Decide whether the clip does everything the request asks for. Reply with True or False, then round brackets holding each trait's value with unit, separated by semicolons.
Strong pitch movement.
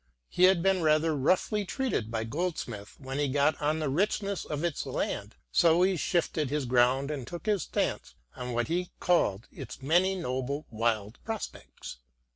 True (5.8 semitones)